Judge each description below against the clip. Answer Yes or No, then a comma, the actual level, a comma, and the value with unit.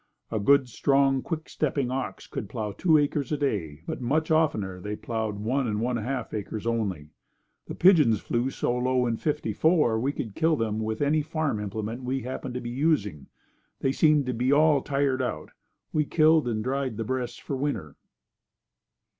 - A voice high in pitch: No, low, 125 Hz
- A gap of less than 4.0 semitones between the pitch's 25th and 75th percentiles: No, average, 4.7 semitones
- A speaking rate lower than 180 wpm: No, average, 185 wpm